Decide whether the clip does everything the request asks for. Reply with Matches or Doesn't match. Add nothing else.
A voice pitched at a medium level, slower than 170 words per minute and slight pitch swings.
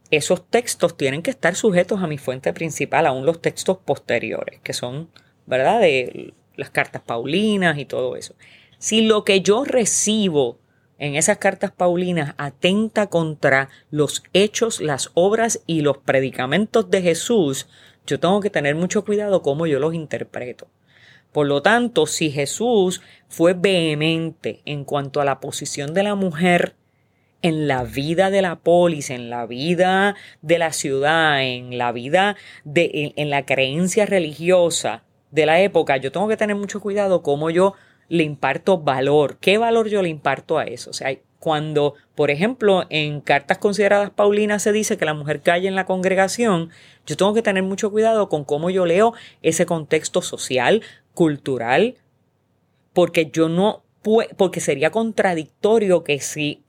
Doesn't match